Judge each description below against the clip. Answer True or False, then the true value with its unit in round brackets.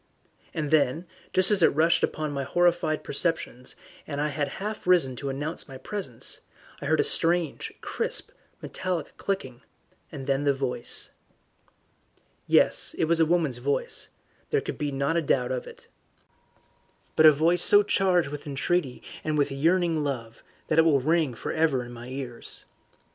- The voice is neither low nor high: True (150 Hz)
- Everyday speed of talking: True (165 wpm)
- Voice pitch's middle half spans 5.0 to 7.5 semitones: False (3.8 semitones)